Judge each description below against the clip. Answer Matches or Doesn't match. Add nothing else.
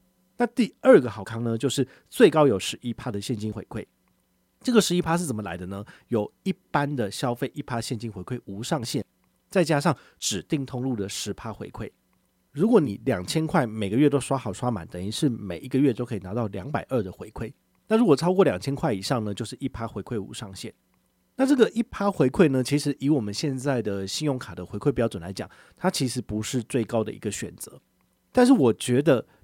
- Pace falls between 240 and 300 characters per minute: Doesn't match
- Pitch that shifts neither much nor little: Doesn't match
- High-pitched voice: Doesn't match